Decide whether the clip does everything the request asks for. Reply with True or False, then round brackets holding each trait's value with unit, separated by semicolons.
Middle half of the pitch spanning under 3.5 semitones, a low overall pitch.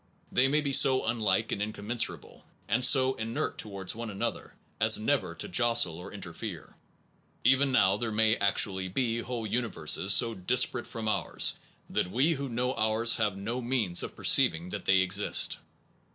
False (4.1 semitones; 110 Hz)